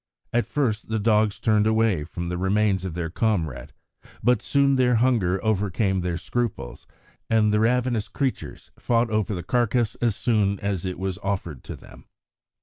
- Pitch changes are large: No, average, 3.8 semitones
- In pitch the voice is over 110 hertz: No, low, 105 Hz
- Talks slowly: No, average, 165 wpm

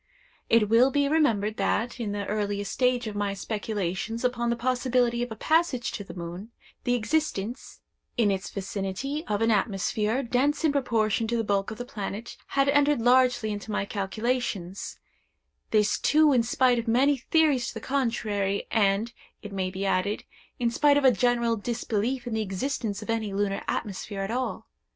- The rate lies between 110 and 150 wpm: No, average, 180 wpm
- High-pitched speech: Yes, high, 230 Hz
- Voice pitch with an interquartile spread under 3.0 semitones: No, average, 3.7 semitones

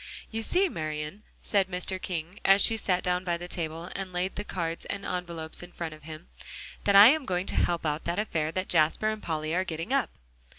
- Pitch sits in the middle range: Yes, medium, 180 Hz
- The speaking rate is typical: No, fast, 215 wpm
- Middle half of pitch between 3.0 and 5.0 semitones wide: Yes, average, 3.3 semitones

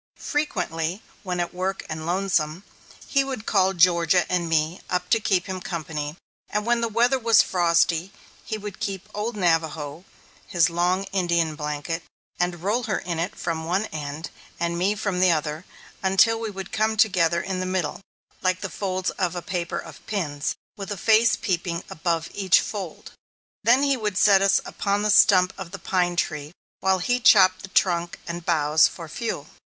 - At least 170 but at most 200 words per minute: Yes, average, 180 wpm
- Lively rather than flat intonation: No, average, 3.2 semitones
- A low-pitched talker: No, medium, 185 Hz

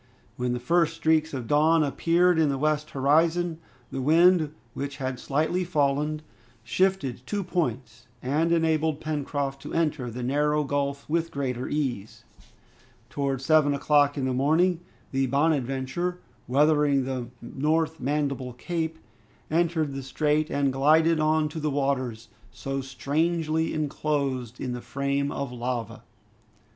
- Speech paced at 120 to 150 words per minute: Yes, slow, 135 wpm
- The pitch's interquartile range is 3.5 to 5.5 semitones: No, average, 3.0 semitones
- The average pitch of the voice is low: No, medium, 145 Hz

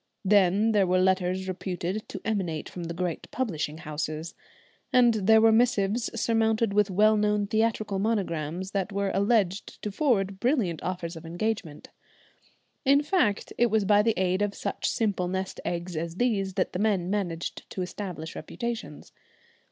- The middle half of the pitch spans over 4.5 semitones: No, average, 3.5 semitones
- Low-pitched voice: No, high, 195 Hz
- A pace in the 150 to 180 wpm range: Yes, average, 160 wpm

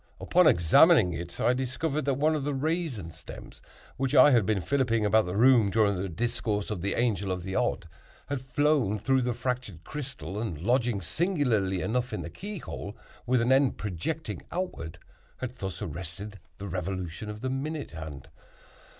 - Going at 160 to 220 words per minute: Yes, average, 175 wpm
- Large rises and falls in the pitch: Yes, wide, 5.8 semitones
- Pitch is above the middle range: No, low, 115 Hz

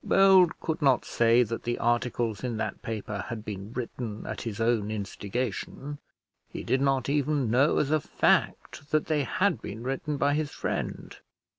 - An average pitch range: Yes, average, 4.4 semitones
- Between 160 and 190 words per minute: Yes, average, 170 wpm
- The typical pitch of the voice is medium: No, low, 125 Hz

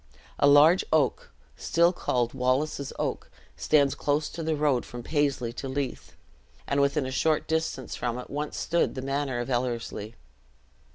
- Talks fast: No, average, 165 wpm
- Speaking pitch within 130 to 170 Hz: Yes, medium, 140 Hz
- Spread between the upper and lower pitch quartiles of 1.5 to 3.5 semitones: Yes, average, 3.1 semitones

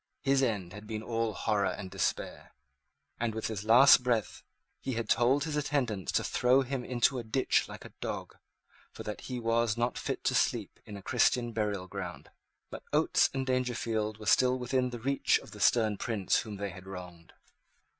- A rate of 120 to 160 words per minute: No, average, 190 wpm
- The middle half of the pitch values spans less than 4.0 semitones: Yes, average, 3.4 semitones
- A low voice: Yes, low, 115 Hz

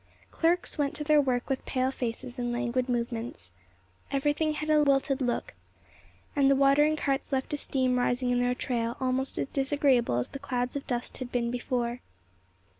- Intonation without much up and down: Yes, narrow, 2.3 semitones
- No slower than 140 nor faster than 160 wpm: No, average, 180 wpm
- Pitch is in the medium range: No, very high, 260 Hz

